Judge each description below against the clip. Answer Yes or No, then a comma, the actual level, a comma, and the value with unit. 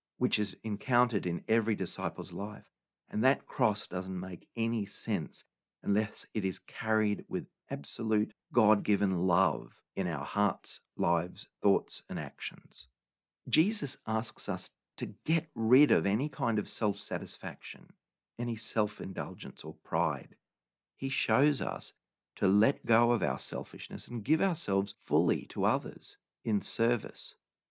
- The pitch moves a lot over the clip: No, average, 3.5 semitones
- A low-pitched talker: Yes, low, 110 Hz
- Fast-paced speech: No, average, 140 wpm